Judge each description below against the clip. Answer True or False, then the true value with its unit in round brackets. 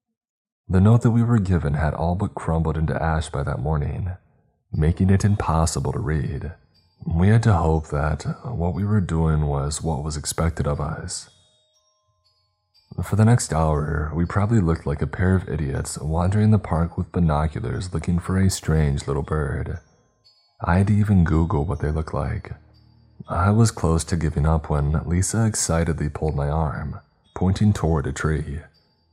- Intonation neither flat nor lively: True (4.7 semitones)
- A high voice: False (85 Hz)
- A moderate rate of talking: True (165 wpm)